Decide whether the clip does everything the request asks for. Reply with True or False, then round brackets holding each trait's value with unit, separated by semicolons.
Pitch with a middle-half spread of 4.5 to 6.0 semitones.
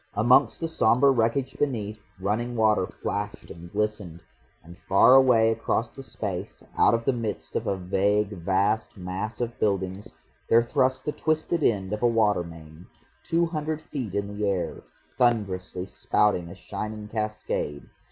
False (3.9 semitones)